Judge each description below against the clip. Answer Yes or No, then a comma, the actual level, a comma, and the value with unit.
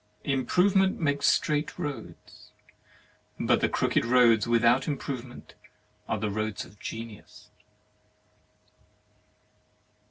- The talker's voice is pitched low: Yes, low, 125 Hz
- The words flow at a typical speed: No, slow, 90 wpm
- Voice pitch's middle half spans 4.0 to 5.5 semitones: Yes, average, 4.3 semitones